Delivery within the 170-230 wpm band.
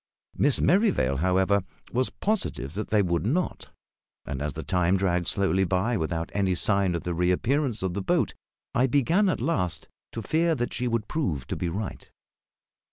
Yes: average, 175 wpm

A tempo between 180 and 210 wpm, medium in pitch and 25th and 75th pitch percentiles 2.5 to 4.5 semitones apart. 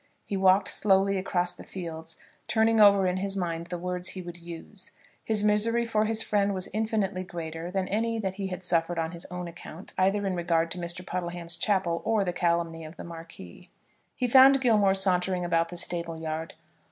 Yes: average, 200 wpm; medium, 180 Hz; average, 2.9 semitones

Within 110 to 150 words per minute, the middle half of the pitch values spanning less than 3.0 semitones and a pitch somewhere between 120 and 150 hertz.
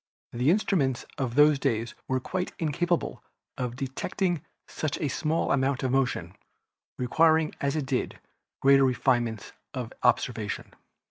No: slow, 135 wpm; average, 3.7 semitones; low, 135 Hz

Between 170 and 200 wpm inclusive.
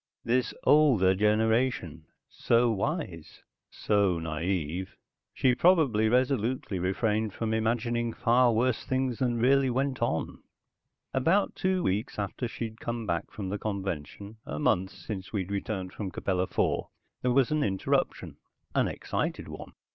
No: slow, 135 wpm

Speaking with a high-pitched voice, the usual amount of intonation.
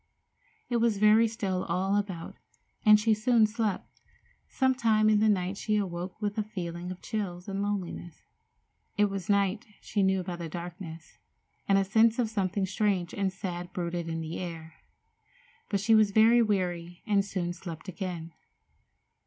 Yes: high, 195 Hz; average, 3.3 semitones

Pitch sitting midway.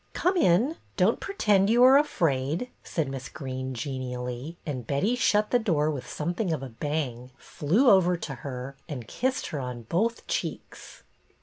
Yes: medium, 150 Hz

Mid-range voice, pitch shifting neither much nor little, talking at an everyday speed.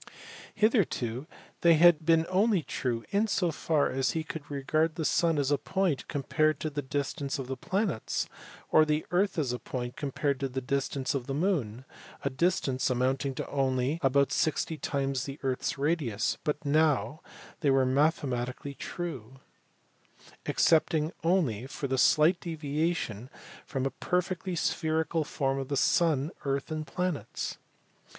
Yes: medium, 145 Hz; average, 3.5 semitones; average, 155 wpm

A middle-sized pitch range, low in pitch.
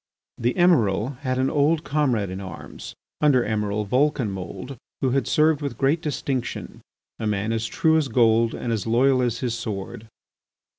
Yes: average, 4.5 semitones; low, 125 Hz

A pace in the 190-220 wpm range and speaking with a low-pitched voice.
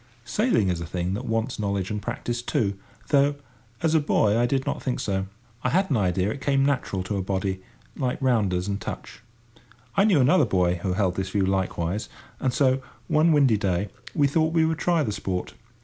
Yes: average, 200 wpm; low, 110 Hz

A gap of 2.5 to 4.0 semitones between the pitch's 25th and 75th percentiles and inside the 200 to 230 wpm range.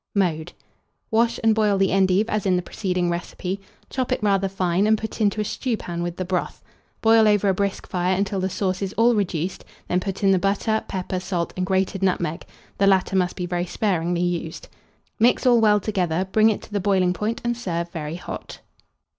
Yes: average, 2.8 semitones; fast, 205 wpm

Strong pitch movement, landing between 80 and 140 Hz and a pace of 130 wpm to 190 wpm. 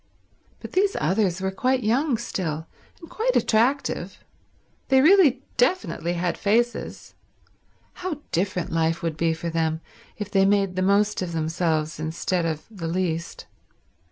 No: wide, 6.5 semitones; high, 190 Hz; average, 140 wpm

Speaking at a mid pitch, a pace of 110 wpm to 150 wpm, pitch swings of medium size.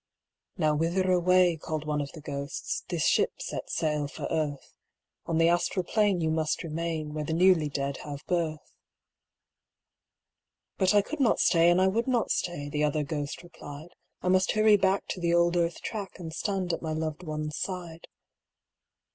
No: medium, 165 Hz; average, 175 wpm; average, 3.2 semitones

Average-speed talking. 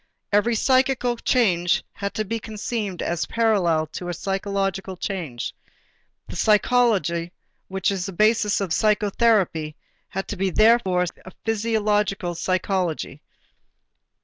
No: slow, 125 wpm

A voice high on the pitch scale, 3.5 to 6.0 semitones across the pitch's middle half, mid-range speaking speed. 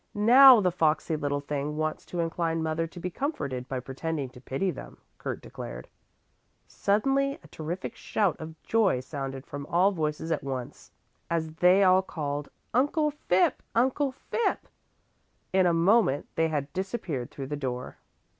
No: medium, 165 Hz; wide, 5.4 semitones; average, 155 wpm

